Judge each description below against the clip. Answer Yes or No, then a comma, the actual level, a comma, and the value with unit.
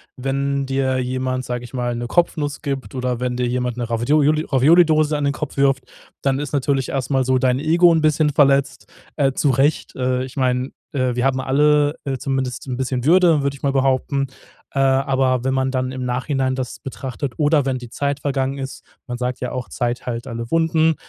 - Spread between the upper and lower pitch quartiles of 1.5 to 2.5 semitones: Yes, narrow, 2.0 semitones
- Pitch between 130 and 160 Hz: Yes, low, 135 Hz